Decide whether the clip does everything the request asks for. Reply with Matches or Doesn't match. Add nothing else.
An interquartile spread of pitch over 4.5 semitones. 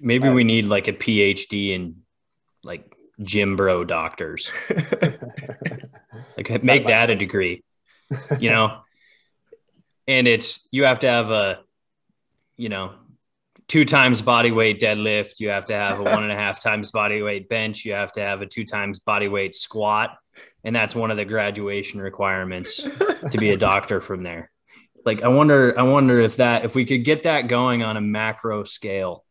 Doesn't match